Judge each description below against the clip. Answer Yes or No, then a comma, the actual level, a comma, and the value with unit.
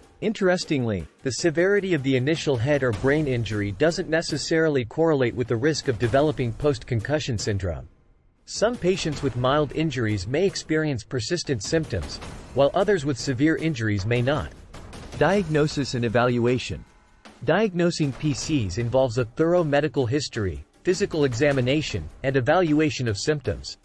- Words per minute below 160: Yes, slow, 135 wpm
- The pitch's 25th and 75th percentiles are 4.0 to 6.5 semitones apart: Yes, average, 4.6 semitones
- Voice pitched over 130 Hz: Yes, medium, 140 Hz